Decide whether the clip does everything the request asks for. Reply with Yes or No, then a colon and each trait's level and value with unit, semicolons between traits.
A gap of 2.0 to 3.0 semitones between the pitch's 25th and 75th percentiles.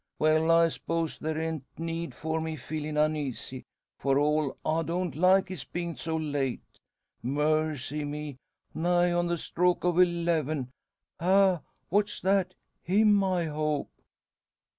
Yes: narrow, 2.5 semitones